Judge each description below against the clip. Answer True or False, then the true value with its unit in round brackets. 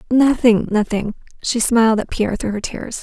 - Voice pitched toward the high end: True (225 Hz)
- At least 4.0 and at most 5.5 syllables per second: True (5.2 syllables/s)